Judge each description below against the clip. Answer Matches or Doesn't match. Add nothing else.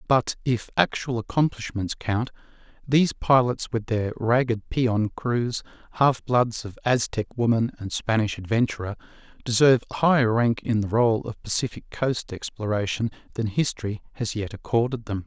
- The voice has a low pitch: Matches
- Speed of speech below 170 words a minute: Matches